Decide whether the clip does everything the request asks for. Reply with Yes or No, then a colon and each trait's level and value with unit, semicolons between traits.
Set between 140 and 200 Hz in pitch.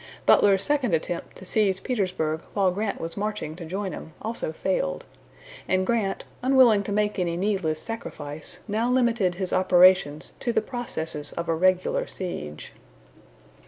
Yes: high, 190 Hz